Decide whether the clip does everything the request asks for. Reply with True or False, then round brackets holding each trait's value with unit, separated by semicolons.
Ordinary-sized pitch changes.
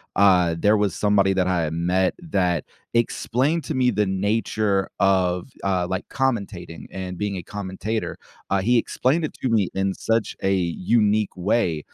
True (3.4 semitones)